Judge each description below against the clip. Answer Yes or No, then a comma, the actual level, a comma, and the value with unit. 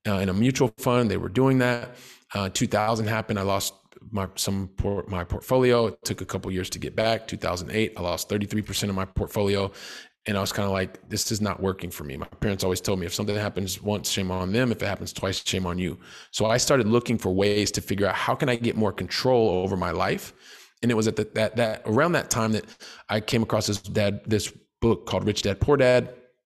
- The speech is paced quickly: Yes, fast, 250 wpm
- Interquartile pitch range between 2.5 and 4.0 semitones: Yes, average, 2.8 semitones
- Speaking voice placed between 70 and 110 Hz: Yes, low, 105 Hz